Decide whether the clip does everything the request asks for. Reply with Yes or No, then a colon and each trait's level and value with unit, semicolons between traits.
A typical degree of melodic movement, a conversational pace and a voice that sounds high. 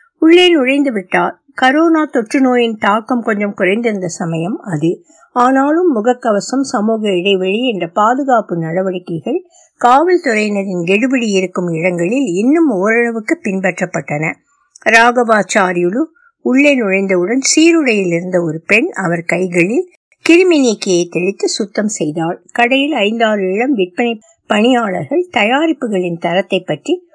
No: wide, 6.9 semitones; average, 85 wpm; high, 225 Hz